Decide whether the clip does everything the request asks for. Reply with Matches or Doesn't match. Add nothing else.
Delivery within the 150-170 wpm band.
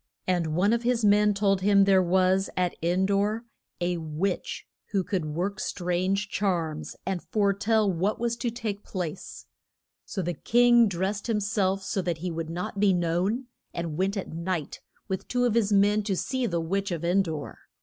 Doesn't match